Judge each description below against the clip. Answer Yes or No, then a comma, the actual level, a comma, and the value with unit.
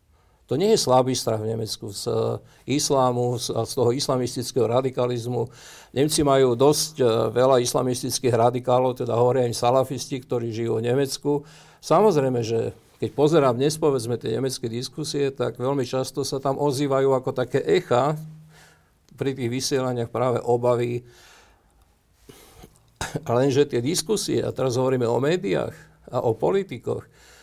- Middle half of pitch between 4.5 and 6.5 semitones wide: No, narrow, 2.6 semitones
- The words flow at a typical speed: Yes, average, 135 wpm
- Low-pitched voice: Yes, low, 130 Hz